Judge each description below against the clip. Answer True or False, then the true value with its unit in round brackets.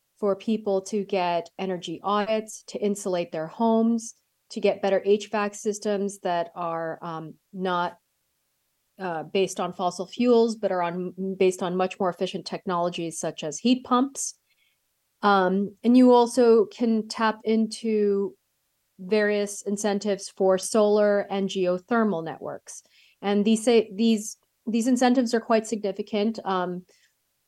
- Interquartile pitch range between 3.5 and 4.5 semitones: False (3.1 semitones)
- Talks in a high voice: True (200 Hz)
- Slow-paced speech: True (130 wpm)